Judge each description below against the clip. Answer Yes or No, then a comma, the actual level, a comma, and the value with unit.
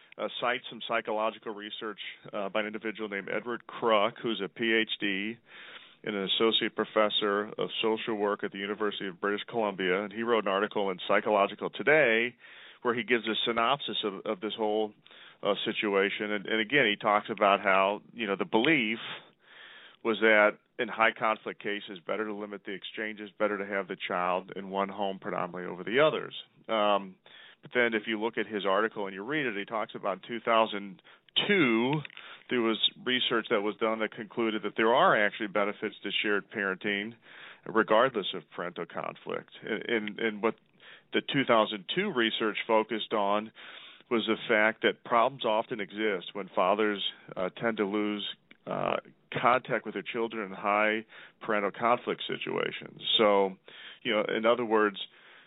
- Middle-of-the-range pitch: No, low, 110 Hz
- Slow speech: No, average, 170 wpm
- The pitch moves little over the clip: Yes, narrow, 1.8 semitones